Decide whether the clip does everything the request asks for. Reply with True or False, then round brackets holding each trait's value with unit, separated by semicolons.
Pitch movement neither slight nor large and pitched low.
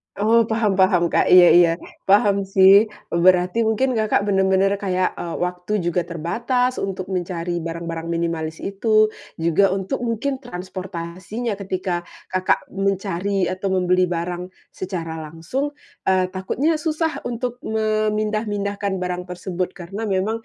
False (3.3 semitones; 190 Hz)